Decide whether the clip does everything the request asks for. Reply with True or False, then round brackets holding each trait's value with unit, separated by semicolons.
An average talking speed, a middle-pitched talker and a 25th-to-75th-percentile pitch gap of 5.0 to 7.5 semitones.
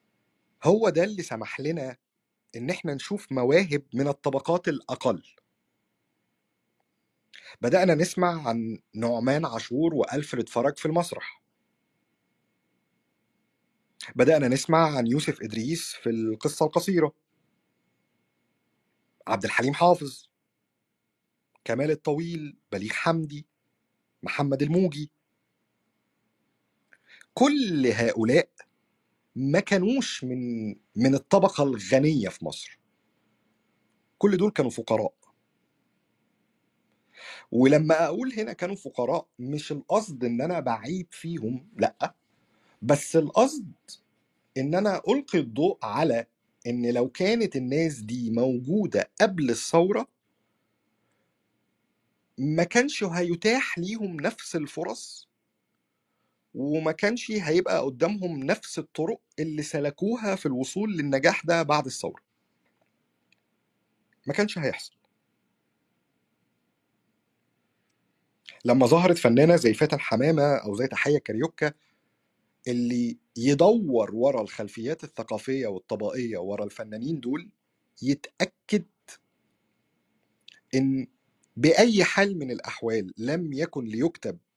True (90 wpm; 150 Hz; 5.6 semitones)